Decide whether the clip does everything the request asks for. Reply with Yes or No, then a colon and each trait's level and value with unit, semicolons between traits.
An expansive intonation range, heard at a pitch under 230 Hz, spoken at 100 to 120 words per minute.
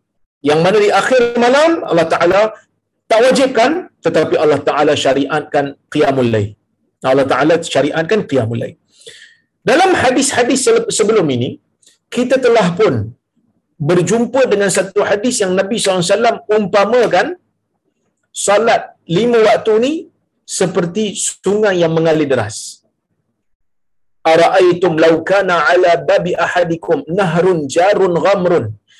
Yes: wide, 6.5 semitones; high, 190 Hz; average, 110 wpm